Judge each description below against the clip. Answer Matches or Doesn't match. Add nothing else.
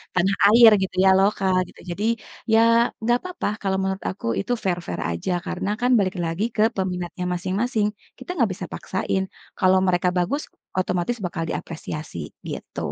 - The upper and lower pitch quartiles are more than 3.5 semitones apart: Doesn't match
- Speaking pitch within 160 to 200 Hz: Matches